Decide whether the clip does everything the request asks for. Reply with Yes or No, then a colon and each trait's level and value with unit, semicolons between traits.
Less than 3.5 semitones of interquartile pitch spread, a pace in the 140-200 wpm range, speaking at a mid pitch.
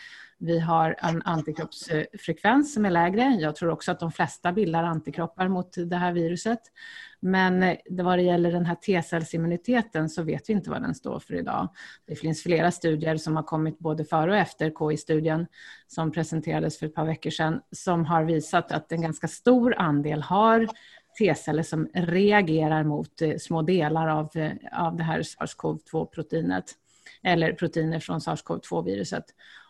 Yes: narrow, 2.5 semitones; average, 155 wpm; medium, 165 Hz